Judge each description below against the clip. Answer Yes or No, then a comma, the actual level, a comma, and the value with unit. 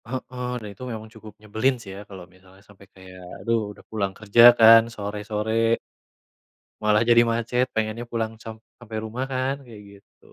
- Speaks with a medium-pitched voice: No, low, 110 Hz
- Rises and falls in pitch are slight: Yes, narrow, 2.3 semitones